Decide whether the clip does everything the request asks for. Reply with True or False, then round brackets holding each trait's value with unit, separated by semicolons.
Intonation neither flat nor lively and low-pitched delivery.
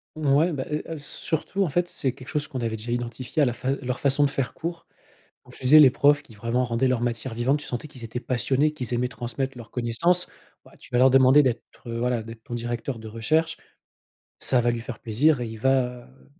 True (3.4 semitones; 125 Hz)